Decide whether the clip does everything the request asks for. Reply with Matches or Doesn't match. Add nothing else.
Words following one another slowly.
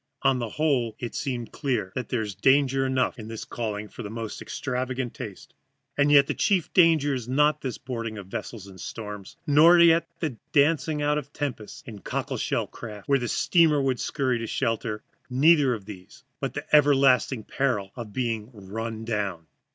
Doesn't match